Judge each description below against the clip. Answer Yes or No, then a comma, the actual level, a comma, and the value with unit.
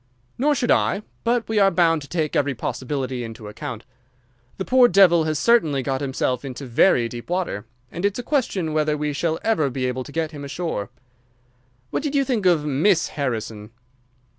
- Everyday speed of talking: Yes, average, 190 wpm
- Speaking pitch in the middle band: Yes, medium, 155 Hz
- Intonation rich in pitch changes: Yes, wide, 6.7 semitones